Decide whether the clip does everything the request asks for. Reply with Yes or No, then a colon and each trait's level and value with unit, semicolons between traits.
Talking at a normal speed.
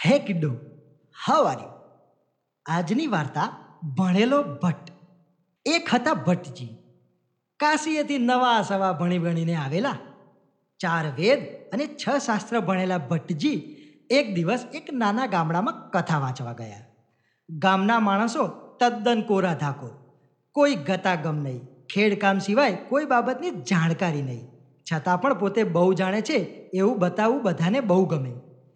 Yes: average, 120 wpm